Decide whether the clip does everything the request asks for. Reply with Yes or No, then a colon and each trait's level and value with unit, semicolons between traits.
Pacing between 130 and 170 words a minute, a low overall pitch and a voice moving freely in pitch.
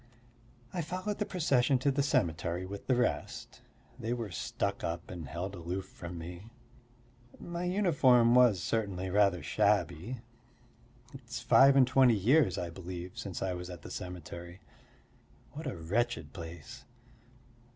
Yes: average, 140 wpm; low, 100 Hz; wide, 6.8 semitones